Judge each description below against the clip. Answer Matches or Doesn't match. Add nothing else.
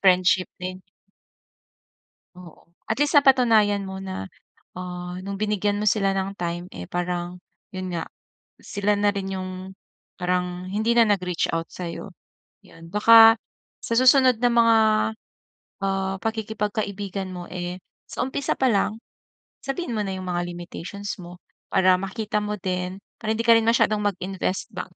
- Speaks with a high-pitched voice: Matches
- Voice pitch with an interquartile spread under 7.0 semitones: Matches